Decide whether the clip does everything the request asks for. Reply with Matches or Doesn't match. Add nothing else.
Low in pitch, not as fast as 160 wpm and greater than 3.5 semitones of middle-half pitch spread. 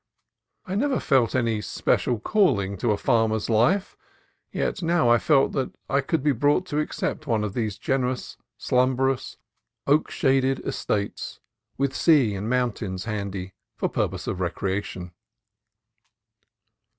Matches